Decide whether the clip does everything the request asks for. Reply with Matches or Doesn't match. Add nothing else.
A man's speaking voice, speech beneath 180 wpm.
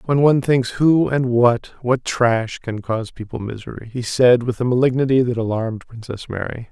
Matches